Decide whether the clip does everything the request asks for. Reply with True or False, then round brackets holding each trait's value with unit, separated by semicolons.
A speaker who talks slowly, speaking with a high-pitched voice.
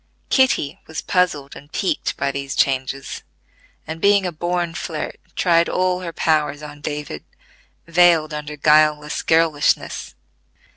False (130 wpm; 155 Hz)